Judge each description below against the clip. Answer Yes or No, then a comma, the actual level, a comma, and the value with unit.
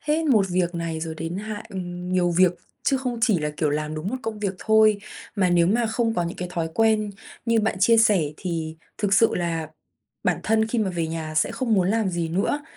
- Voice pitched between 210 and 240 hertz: No, high, 190 Hz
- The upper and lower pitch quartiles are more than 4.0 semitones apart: Yes, average, 4.6 semitones